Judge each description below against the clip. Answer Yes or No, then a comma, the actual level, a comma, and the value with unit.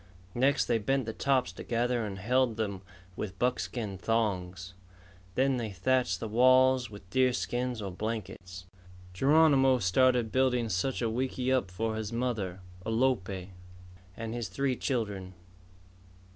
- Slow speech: Yes, slow, 130 wpm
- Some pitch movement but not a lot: Yes, average, 4.5 semitones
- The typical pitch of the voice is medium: No, low, 115 Hz